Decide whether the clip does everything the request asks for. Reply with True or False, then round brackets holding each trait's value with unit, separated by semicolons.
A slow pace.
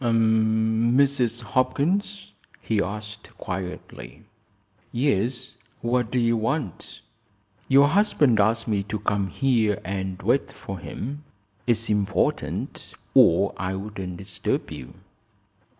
True (105 wpm)